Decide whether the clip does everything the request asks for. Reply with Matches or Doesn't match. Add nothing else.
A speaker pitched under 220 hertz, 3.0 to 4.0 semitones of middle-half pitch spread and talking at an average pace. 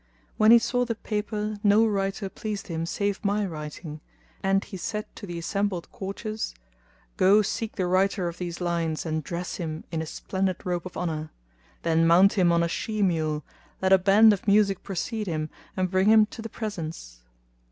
Matches